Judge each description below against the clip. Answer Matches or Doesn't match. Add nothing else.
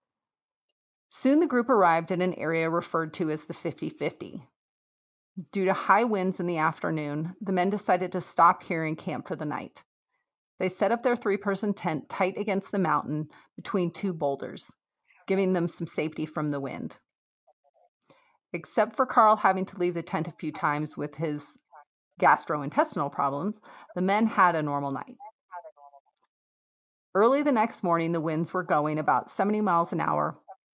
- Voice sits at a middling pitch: Matches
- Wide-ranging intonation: Doesn't match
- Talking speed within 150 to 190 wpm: Matches